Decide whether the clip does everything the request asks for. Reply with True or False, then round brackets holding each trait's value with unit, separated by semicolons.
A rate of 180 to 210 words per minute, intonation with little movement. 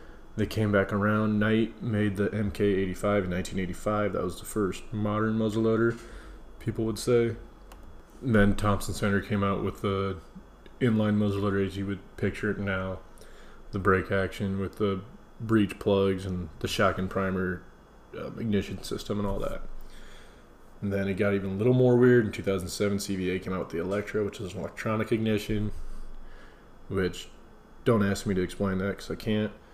False (170 wpm; 2.0 semitones)